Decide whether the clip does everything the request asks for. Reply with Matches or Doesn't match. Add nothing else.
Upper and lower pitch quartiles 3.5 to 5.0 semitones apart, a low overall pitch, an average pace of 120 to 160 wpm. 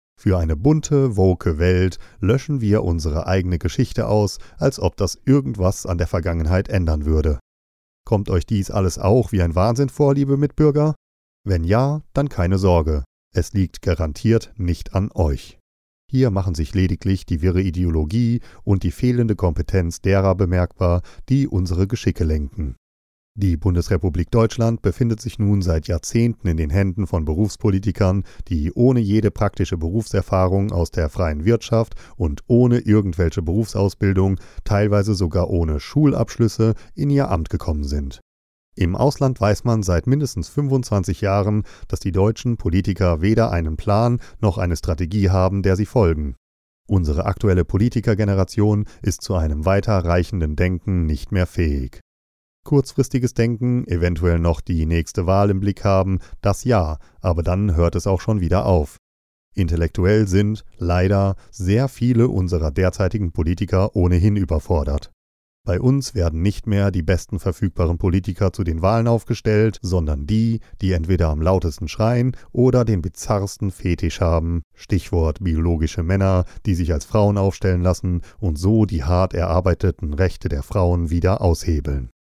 Matches